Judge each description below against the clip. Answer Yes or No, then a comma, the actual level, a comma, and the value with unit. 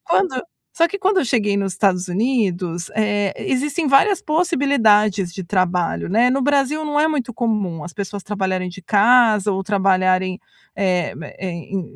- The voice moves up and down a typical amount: No, wide, 6.3 semitones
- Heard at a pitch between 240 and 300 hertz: No, high, 205 Hz